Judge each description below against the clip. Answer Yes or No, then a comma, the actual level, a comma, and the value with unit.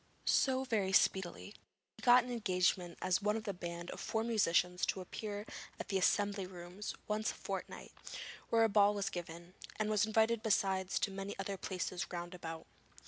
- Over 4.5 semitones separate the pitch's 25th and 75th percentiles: No, average, 3.2 semitones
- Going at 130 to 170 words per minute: No, average, 180 wpm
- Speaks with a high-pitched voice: Yes, high, 195 Hz